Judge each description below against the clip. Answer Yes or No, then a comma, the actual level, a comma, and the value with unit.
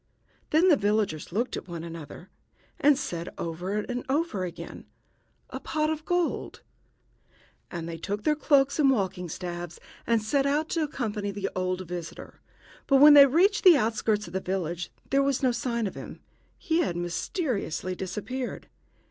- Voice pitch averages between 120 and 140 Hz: No, high, 215 Hz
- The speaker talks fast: No, average, 160 wpm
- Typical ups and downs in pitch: No, wide, 7.7 semitones